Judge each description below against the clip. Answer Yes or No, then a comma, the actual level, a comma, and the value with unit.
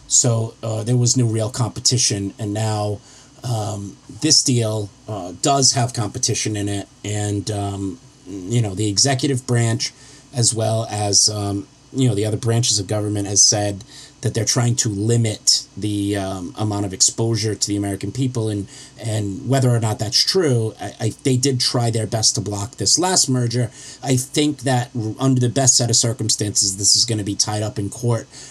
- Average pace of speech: Yes, average, 185 wpm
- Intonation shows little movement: No, average, 3.8 semitones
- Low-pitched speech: Yes, low, 115 Hz